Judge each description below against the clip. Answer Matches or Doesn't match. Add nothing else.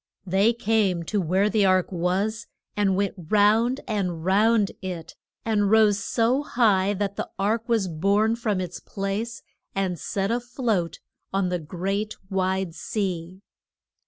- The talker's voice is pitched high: Matches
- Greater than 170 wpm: Doesn't match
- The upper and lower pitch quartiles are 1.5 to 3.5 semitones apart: Matches